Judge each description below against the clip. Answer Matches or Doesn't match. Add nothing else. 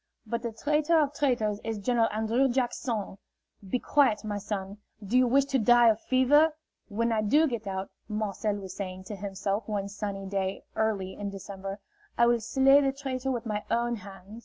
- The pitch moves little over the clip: Doesn't match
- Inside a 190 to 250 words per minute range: Matches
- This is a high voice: Matches